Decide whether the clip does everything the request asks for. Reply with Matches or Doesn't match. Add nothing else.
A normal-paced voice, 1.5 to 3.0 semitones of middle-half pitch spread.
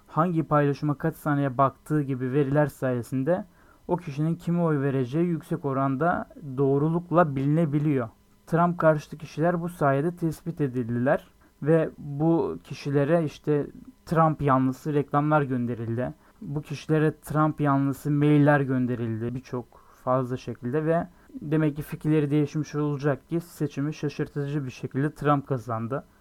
Matches